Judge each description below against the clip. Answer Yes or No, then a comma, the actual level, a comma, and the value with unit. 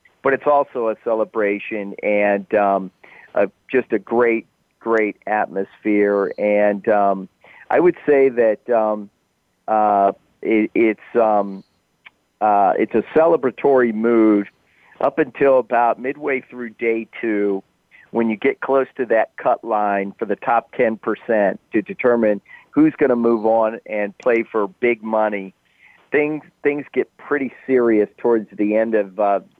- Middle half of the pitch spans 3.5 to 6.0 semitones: No, average, 2.9 semitones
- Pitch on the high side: No, low, 110 Hz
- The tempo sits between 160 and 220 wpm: No, average, 145 wpm